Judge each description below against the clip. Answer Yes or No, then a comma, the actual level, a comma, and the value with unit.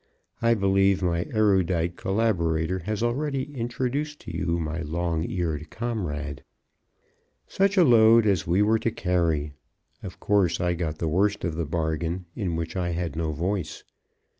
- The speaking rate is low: No, average, 155 wpm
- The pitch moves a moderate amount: Yes, average, 4.7 semitones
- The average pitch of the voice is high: No, very low, 90 Hz